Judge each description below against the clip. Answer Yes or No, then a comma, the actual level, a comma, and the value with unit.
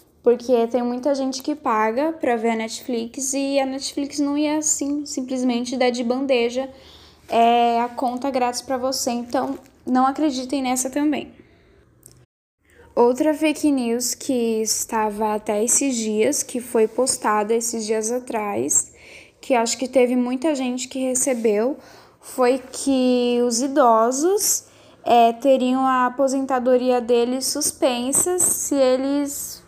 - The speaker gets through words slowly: No, average, 130 wpm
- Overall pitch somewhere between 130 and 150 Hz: No, very high, 255 Hz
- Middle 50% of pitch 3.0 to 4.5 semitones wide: No, narrow, 2.5 semitones